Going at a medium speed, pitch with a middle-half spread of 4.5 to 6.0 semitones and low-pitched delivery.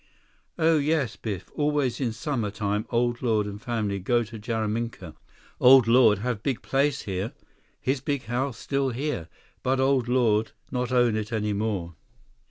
No: average, 160 wpm; average, 3.8 semitones; low, 120 Hz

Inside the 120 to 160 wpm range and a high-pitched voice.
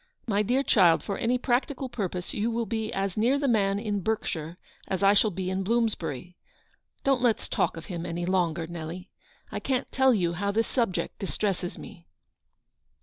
No: average, 180 wpm; high, 200 Hz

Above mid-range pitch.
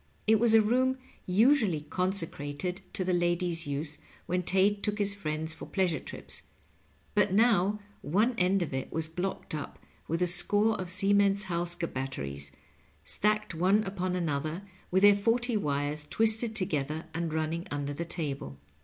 No: medium, 180 Hz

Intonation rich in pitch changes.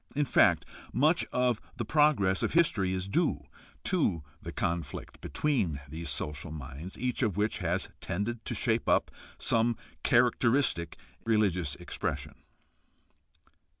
Yes: wide, 6.5 semitones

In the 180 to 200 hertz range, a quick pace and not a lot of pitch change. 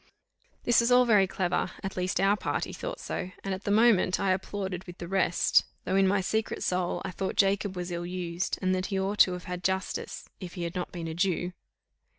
Yes: medium, 185 Hz; fast, 225 wpm; narrow, 1.6 semitones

